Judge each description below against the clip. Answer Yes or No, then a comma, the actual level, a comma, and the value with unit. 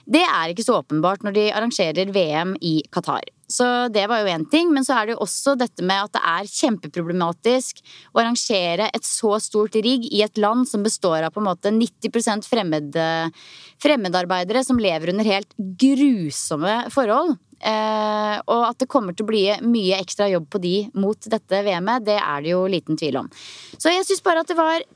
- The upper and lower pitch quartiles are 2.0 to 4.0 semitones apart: No, average, 4.5 semitones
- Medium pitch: No, high, 210 Hz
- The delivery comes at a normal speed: Yes, average, 195 wpm